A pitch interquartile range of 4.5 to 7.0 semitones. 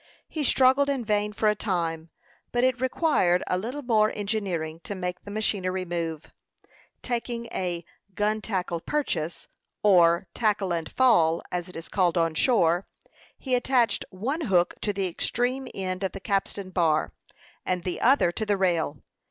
Yes: average, 5.0 semitones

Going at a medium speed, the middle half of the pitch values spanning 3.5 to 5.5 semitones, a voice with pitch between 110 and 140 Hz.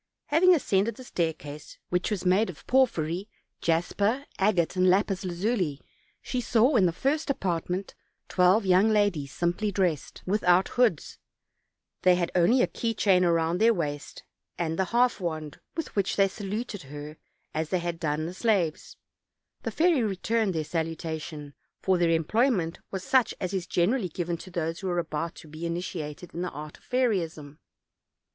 No: average, 165 wpm; average, 4.4 semitones; medium, 180 Hz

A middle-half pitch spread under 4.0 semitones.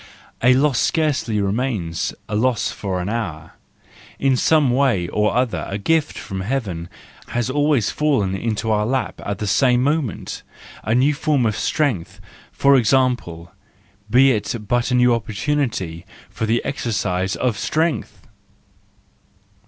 No: average, 5.1 semitones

